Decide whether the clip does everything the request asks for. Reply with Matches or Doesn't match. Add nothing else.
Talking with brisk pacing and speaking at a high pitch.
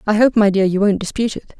Matches